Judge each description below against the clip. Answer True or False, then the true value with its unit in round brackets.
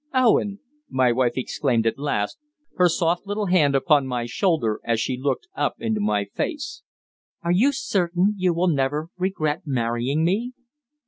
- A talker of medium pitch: True (160 Hz)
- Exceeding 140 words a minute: True (155 wpm)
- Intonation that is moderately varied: False (6.8 semitones)